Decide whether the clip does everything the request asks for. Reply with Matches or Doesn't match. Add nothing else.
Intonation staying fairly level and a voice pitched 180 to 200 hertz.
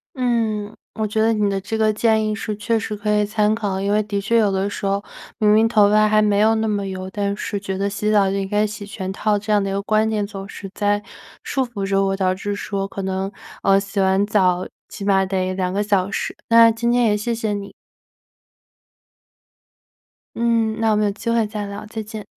Doesn't match